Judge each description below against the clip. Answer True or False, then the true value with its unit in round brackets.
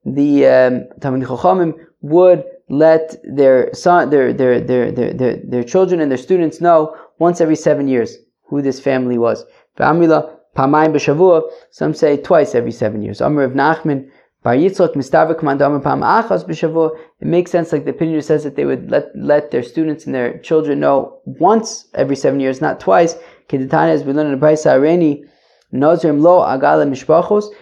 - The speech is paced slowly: True (120 wpm)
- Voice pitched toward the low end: False (155 Hz)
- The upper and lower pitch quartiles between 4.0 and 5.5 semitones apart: False (3.3 semitones)